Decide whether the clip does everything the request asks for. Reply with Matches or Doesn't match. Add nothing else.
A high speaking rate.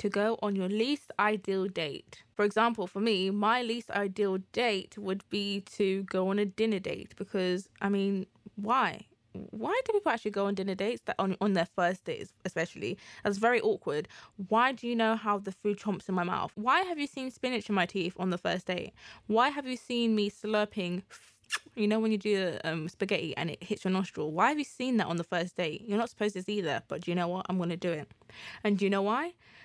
Matches